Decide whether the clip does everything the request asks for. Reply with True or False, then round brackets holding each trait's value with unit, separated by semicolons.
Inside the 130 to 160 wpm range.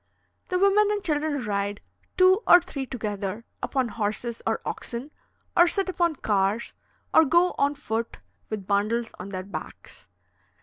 True (145 wpm)